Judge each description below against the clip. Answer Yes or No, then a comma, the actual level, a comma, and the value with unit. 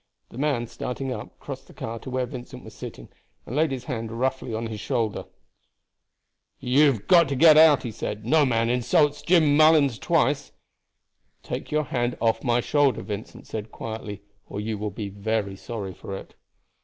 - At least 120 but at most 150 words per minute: No, average, 180 wpm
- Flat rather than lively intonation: No, average, 4.5 semitones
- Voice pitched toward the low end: Yes, low, 120 Hz